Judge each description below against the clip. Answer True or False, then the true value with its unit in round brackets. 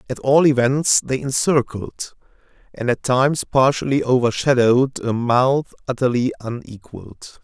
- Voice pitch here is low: True (130 Hz)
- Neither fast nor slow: False (115 wpm)